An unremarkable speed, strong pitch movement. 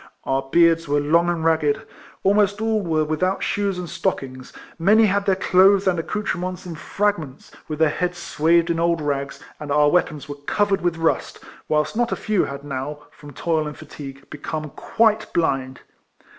No: average, 180 wpm; average, 4.3 semitones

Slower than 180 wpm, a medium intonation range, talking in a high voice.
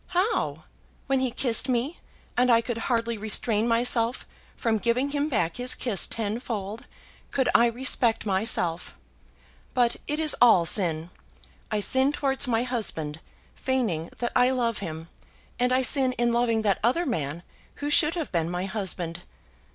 Yes: average, 155 wpm; average, 4.1 semitones; high, 235 Hz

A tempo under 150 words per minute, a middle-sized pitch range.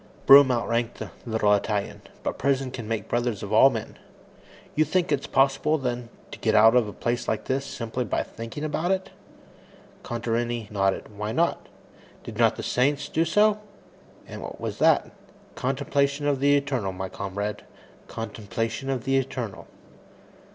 No: average, 160 wpm; average, 4.0 semitones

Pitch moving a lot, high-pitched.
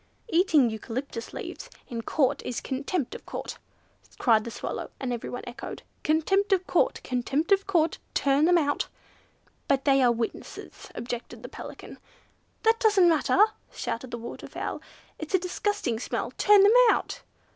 Yes: wide, 7.5 semitones; very high, 285 Hz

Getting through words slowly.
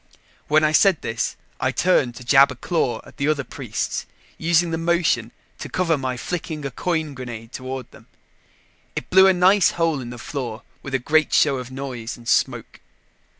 No: average, 190 wpm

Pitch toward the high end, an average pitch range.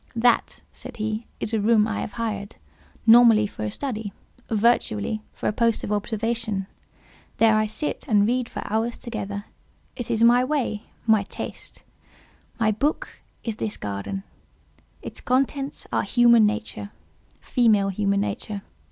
No: high, 220 Hz; narrow, 2.3 semitones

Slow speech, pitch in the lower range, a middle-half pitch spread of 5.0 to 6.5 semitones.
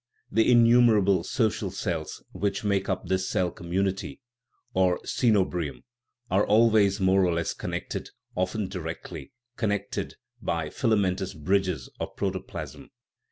No: slow, 125 wpm; very low, 95 Hz; narrow, 2.5 semitones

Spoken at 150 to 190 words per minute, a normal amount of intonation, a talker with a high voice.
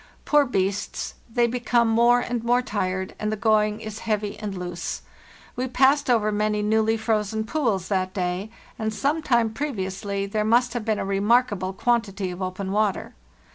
Yes: average, 170 wpm; average, 3.2 semitones; high, 215 Hz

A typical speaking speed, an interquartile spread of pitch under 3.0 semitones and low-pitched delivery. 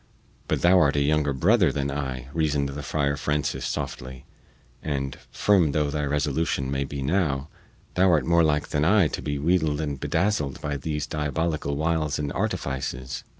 Yes: average, 170 wpm; narrow, 2.4 semitones; very low, 75 Hz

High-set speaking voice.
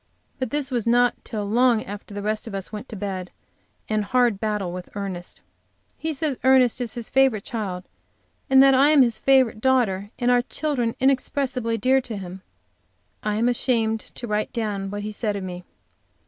Yes: high, 225 Hz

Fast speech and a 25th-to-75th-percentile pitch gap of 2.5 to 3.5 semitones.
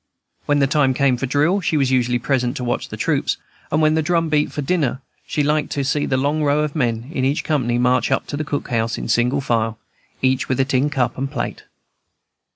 Yes: fast, 225 wpm; average, 3.0 semitones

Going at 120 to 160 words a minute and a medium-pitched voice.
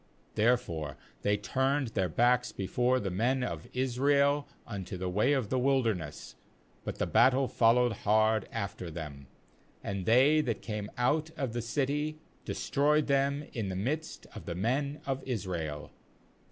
No: average, 150 wpm; low, 120 Hz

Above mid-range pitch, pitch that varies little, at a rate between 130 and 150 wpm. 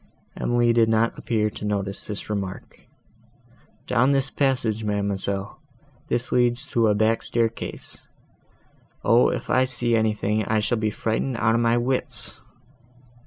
No: low, 115 Hz; narrow, 2.1 semitones; average, 140 wpm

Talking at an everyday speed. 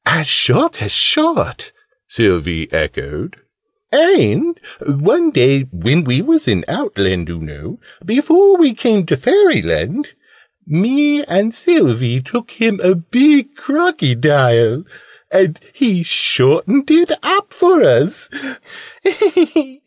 No: slow, 110 wpm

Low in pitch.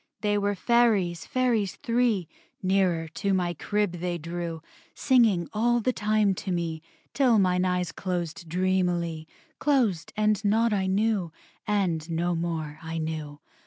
No: medium, 185 Hz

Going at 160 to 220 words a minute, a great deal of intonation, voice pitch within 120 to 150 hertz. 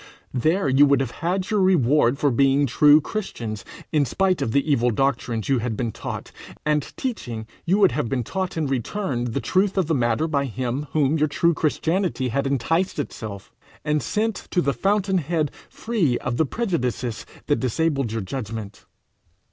Yes: average, 180 wpm; wide, 5.7 semitones; medium, 140 Hz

